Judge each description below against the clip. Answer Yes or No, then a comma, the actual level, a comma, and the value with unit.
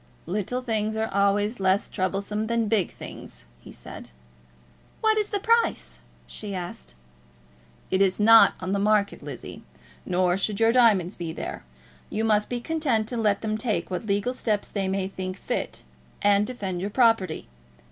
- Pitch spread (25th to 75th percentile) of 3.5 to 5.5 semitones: No, average, 2.9 semitones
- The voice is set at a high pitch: Yes, high, 210 Hz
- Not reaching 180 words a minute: Yes, average, 165 wpm